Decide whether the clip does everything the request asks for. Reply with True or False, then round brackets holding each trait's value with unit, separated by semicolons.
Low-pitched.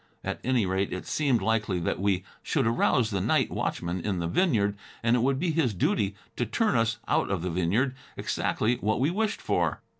True (110 Hz)